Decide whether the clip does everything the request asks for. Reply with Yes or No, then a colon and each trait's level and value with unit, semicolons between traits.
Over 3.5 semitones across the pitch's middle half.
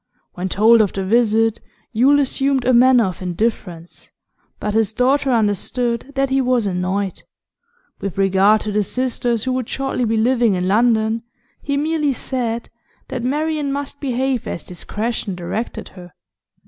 Yes: average, 4.2 semitones